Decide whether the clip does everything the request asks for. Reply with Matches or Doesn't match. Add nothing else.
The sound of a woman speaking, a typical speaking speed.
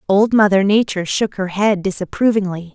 Matches